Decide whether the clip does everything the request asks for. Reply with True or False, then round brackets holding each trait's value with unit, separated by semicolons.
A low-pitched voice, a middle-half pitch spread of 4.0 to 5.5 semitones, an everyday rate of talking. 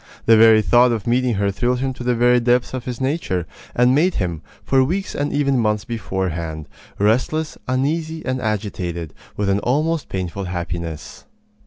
True (120 Hz; 5.1 semitones; 170 wpm)